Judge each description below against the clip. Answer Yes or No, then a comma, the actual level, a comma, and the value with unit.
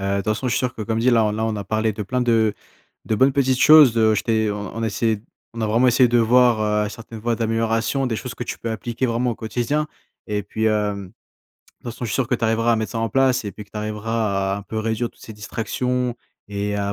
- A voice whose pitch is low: Yes, low, 115 Hz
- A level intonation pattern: Yes, narrow, 2.2 semitones